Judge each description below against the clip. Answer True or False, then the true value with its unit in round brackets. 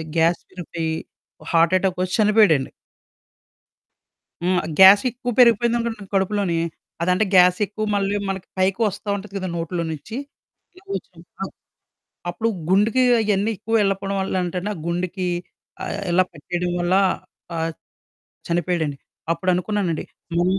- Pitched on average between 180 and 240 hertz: True (185 Hz)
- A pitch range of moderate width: True (3.0 semitones)